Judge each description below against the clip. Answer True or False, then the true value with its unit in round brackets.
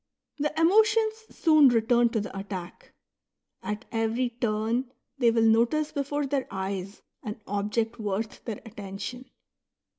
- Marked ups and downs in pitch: False (4.8 semitones)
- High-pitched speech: True (230 Hz)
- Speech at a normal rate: False (125 wpm)